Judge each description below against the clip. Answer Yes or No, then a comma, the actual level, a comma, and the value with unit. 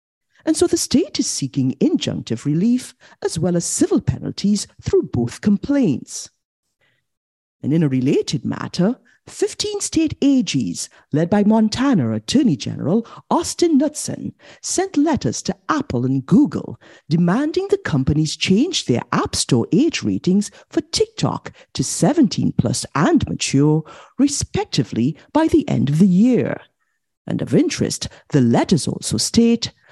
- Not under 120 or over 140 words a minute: Yes, slow, 135 wpm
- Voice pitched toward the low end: No, high, 220 Hz